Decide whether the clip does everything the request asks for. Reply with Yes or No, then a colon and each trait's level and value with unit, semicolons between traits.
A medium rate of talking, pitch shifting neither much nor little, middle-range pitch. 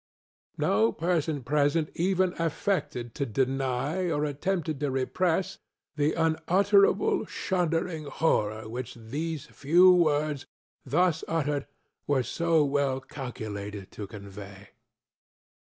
No: slow, 105 wpm; average, 4.7 semitones; medium, 145 Hz